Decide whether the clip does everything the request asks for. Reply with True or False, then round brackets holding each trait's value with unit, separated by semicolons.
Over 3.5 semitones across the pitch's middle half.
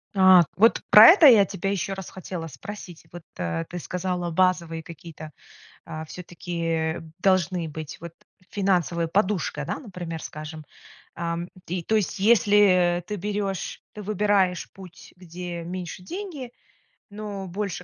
False (3.0 semitones)